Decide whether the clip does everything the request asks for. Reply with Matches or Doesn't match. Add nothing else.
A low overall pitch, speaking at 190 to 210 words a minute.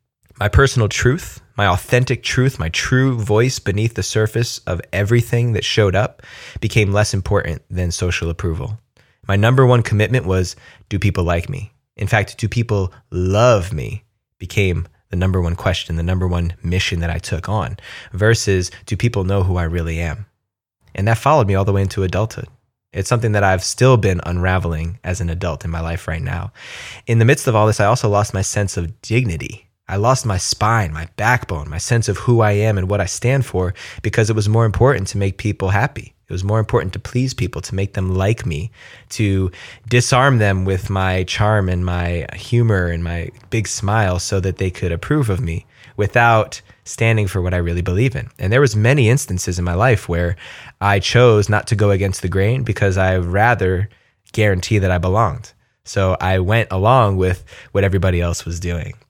Matches